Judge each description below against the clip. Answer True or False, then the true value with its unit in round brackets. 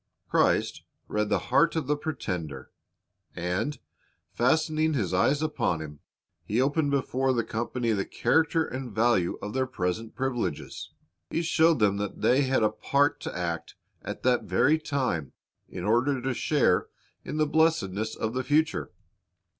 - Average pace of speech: True (155 wpm)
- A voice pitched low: True (125 Hz)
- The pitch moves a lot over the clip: True (6.1 semitones)